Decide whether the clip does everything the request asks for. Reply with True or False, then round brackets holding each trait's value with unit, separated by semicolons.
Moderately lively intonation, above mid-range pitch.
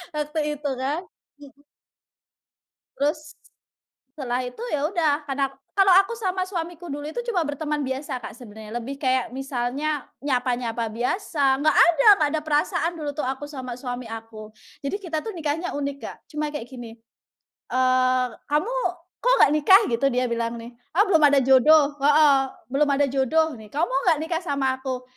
True (3.3 semitones; 280 Hz)